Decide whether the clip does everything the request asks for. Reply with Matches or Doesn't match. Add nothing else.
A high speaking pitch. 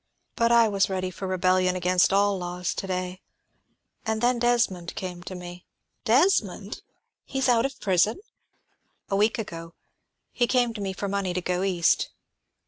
Matches